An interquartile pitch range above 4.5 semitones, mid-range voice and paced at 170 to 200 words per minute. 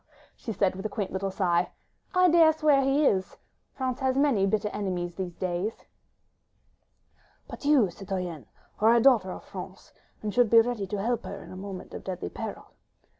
No: average, 5.1 semitones; high, 205 Hz; average, 185 wpm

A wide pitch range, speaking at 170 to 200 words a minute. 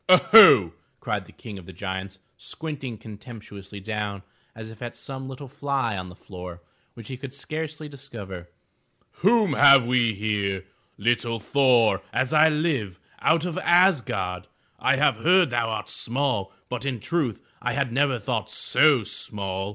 No: wide, 5.8 semitones; average, 155 wpm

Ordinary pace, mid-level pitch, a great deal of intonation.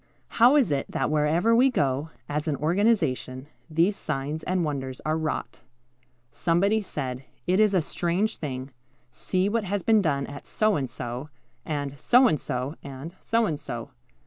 Yes: average, 170 wpm; medium, 155 Hz; wide, 6.4 semitones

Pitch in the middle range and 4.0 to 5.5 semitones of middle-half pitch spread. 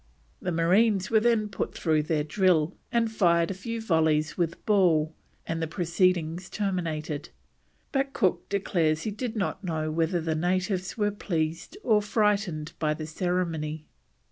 Yes: medium, 175 Hz; average, 4.5 semitones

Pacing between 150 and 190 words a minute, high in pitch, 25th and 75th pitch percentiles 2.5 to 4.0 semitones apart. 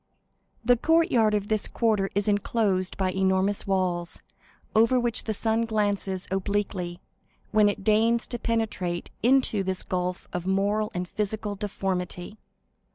No: slow, 135 wpm; high, 205 Hz; average, 2.8 semitones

